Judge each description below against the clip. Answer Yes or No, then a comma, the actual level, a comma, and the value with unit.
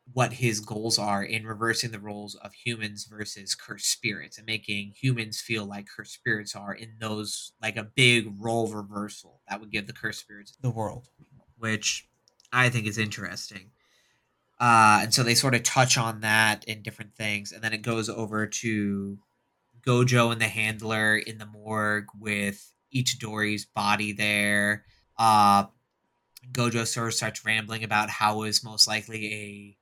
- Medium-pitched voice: No, low, 110 Hz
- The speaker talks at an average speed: Yes, average, 165 wpm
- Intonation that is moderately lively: No, narrow, 1.7 semitones